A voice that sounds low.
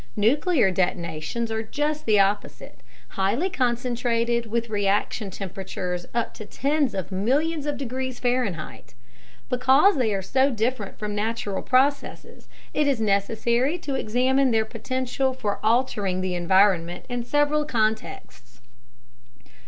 No: high, 230 Hz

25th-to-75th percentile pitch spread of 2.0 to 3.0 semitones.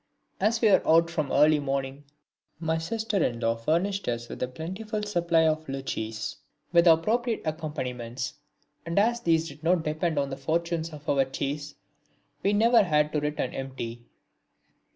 No: average, 4.1 semitones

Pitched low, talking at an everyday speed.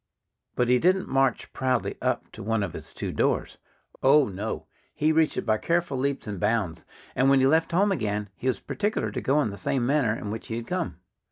No: low, 130 Hz; fast, 225 wpm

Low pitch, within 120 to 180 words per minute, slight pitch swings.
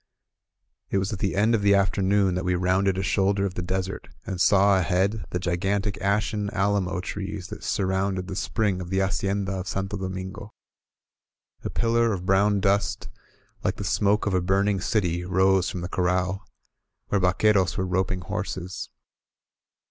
Yes: very low, 95 Hz; average, 170 wpm; narrow, 1.6 semitones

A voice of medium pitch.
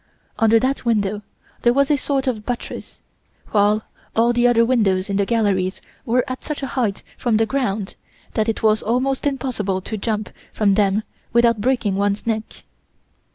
No: high, 225 Hz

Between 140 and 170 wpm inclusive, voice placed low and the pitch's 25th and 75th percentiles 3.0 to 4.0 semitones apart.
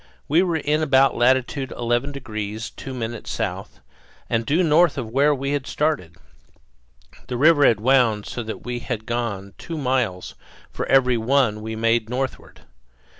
Yes: average, 160 wpm; low, 125 Hz; average, 3.7 semitones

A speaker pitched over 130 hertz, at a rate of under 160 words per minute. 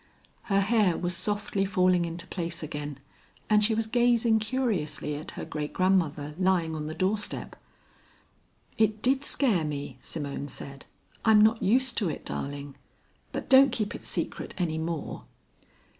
Yes: medium, 185 Hz; average, 150 wpm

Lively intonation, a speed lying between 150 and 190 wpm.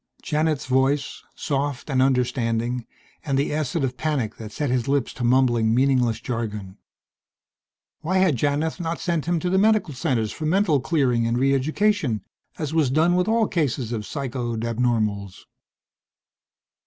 No: average, 4.7 semitones; average, 155 wpm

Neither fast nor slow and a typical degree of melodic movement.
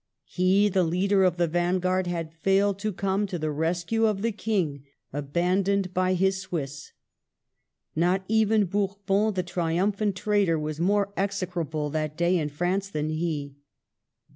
Yes: average, 145 wpm; average, 3.3 semitones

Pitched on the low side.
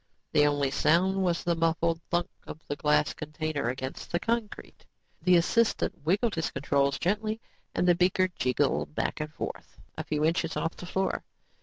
No: medium, 165 Hz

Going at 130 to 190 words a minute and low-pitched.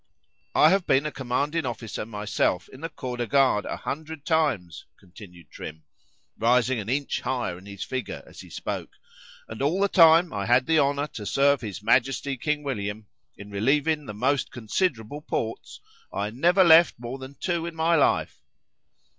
Yes: average, 170 wpm; low, 130 Hz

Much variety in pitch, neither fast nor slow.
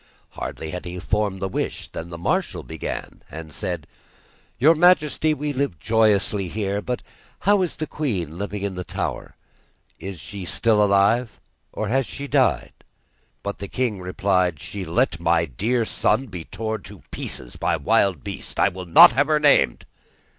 Yes: wide, 5.8 semitones; average, 170 wpm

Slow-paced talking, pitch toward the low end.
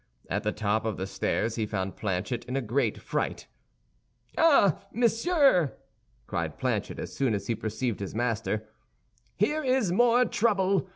No: average, 155 wpm; low, 125 Hz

